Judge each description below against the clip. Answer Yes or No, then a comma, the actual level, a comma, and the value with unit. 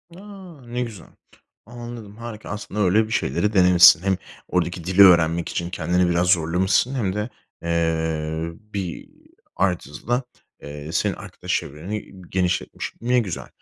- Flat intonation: No, average, 4.1 semitones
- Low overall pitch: Yes, very low, 90 Hz